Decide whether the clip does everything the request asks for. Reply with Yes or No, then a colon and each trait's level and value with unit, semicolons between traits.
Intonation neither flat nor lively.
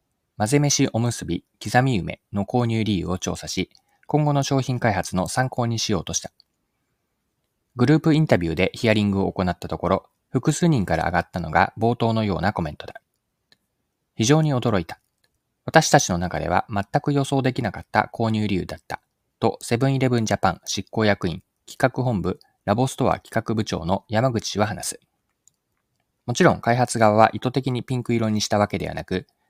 Yes: average, 5.0 semitones